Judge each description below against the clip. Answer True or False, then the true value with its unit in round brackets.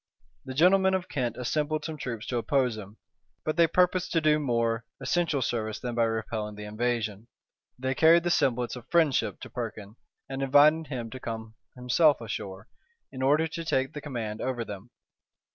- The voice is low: True (130 Hz)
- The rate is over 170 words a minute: True (180 wpm)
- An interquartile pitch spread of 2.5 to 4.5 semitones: False (5.1 semitones)